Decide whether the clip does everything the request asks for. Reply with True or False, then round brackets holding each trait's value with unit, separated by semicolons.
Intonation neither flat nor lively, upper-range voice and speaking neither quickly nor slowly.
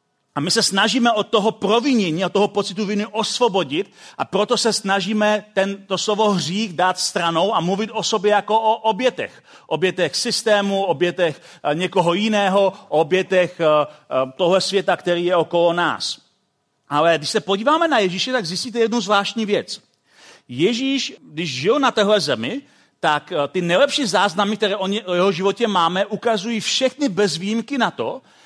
True (3.5 semitones; 200 Hz; 160 wpm)